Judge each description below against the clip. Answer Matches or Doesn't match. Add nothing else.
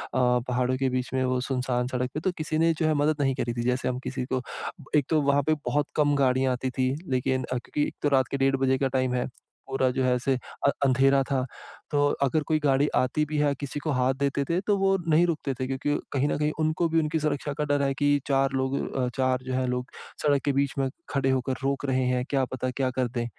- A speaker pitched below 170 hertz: Matches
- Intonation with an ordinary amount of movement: Doesn't match